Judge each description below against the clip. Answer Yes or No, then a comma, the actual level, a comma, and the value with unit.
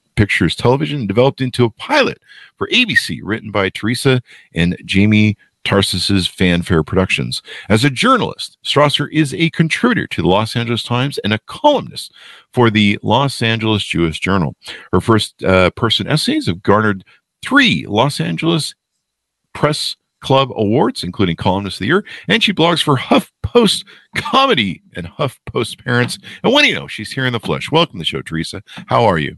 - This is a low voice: Yes, low, 115 Hz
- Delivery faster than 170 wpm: No, average, 165 wpm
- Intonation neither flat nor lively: No, wide, 6.8 semitones